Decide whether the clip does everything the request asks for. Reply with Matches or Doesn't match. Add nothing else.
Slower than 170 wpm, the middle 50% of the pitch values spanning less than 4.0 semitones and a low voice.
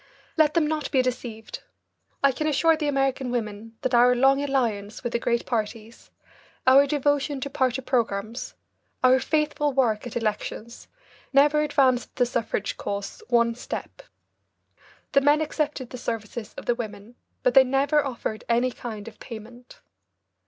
Doesn't match